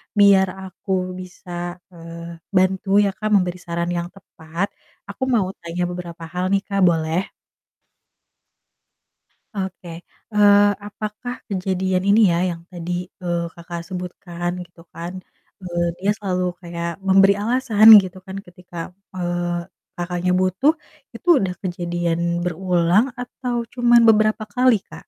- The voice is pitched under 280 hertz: Yes, medium, 185 Hz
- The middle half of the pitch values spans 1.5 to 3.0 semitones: Yes, narrow, 2.4 semitones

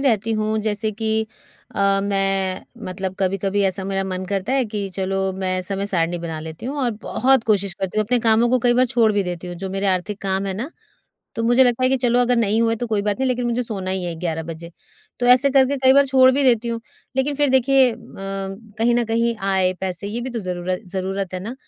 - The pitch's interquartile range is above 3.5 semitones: Yes, average, 4.2 semitones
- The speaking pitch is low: No, high, 210 Hz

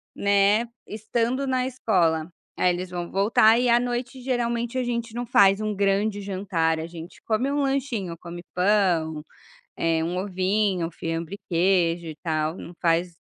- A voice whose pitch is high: Yes, high, 195 Hz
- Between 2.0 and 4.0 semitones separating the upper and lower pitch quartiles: No, wide, 5.4 semitones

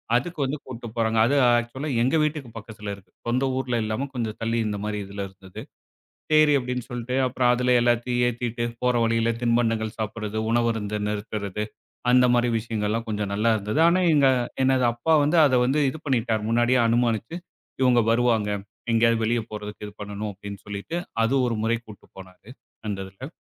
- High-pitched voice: No, low, 115 Hz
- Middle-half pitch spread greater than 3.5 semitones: No, average, 2.9 semitones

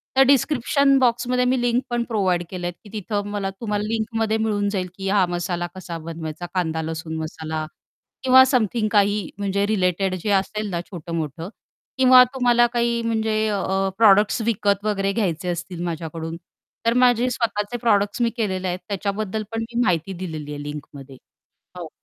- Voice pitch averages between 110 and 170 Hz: No, high, 205 Hz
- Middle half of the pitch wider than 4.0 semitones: Yes, average, 4.7 semitones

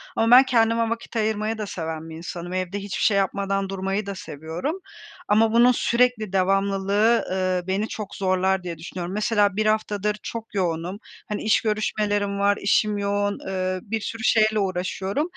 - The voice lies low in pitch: No, high, 200 Hz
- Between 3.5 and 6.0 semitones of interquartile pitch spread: No, narrow, 2.5 semitones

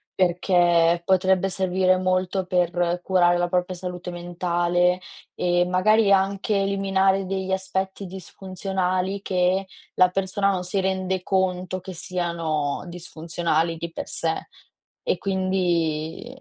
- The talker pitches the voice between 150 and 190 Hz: Yes, medium, 185 Hz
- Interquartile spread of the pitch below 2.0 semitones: Yes, narrow, 1.4 semitones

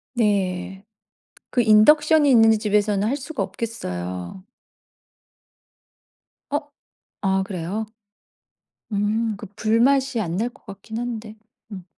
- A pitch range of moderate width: Yes, average, 3.7 semitones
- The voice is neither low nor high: No, high, 215 Hz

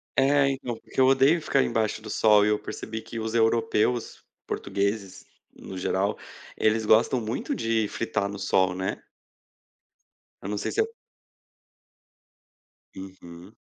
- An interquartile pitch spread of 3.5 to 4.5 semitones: No, average, 2.9 semitones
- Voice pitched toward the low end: Yes, low, 110 Hz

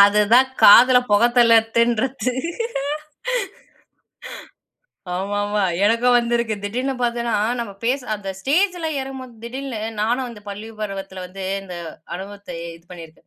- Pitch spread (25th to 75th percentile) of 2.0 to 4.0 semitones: Yes, average, 3.5 semitones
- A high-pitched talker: Yes, high, 230 Hz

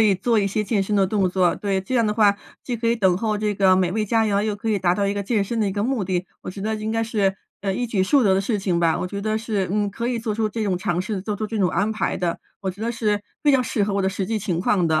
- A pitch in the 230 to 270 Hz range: No, high, 205 Hz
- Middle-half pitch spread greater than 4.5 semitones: No, narrow, 2.5 semitones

